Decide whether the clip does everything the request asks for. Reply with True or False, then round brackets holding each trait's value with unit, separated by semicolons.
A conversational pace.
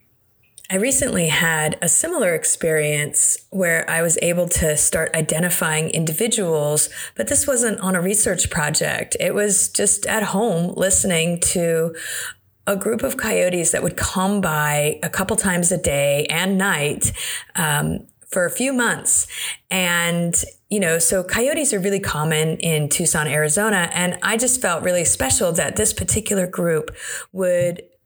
True (150 wpm)